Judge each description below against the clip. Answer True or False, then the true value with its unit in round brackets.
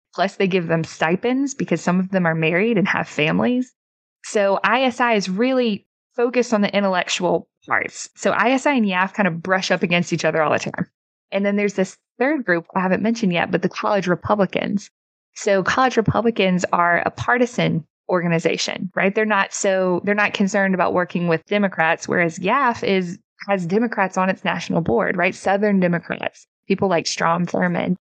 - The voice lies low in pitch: False (190 Hz)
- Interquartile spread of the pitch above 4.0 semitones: False (3.2 semitones)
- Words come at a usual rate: True (180 wpm)